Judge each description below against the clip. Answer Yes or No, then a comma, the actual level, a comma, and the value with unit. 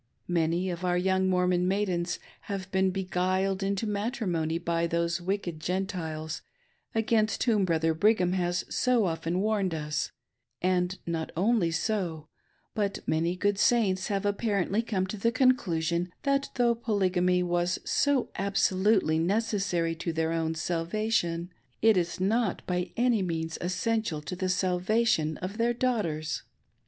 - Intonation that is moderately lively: Yes, average, 3.5 semitones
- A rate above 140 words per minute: No, slow, 135 wpm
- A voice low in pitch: No, medium, 185 Hz